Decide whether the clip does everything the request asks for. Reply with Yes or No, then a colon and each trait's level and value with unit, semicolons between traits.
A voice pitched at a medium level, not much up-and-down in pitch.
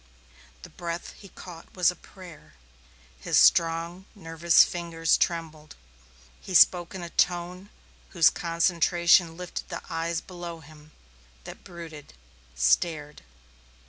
Yes: medium, 170 Hz; narrow, 1.4 semitones